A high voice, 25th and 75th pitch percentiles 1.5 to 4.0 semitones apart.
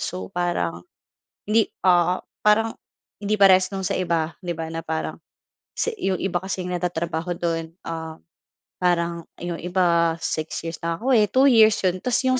No: medium, 175 Hz; average, 2.8 semitones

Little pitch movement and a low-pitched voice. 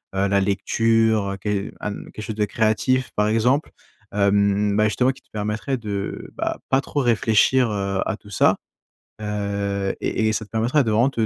Yes: narrow, 2.1 semitones; low, 105 Hz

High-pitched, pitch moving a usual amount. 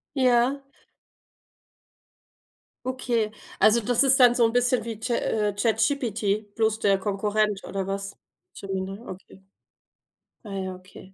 Yes: high, 215 Hz; average, 3.4 semitones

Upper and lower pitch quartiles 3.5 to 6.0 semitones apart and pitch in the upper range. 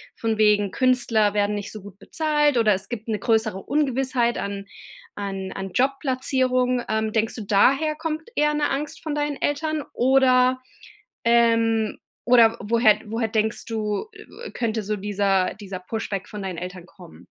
Yes: average, 4.0 semitones; high, 225 Hz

